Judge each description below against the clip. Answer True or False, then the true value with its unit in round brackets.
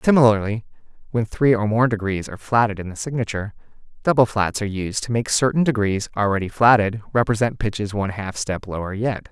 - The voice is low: True (110 Hz)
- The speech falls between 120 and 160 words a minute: False (180 wpm)